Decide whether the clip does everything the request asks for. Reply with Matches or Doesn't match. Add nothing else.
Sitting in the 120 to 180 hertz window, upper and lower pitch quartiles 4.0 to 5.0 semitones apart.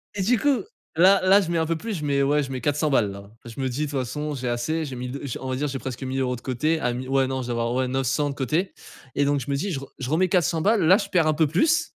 Matches